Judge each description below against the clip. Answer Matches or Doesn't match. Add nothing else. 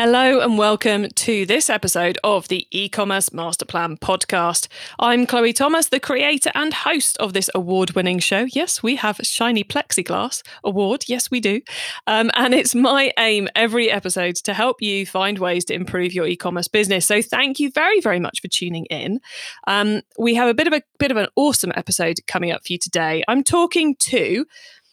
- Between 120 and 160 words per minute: Doesn't match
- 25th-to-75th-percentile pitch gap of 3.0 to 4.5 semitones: Doesn't match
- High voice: Matches